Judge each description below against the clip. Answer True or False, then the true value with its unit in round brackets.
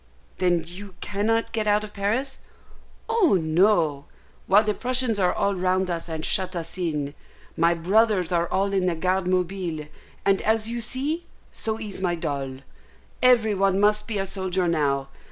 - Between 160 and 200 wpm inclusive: True (165 wpm)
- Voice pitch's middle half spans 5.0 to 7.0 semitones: False (3.8 semitones)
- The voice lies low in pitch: False (190 Hz)